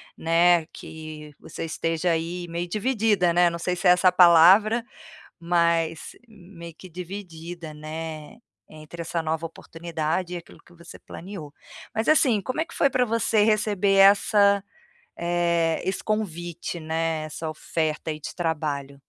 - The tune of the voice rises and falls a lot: No, average, 3.2 semitones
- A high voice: No, medium, 170 Hz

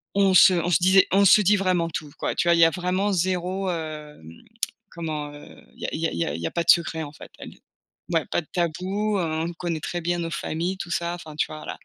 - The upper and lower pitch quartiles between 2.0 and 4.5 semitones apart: Yes, average, 2.7 semitones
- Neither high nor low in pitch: Yes, medium, 170 Hz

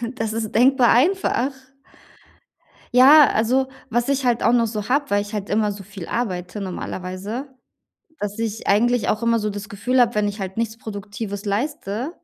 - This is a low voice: No, high, 220 Hz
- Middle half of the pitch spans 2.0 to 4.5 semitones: Yes, average, 3.3 semitones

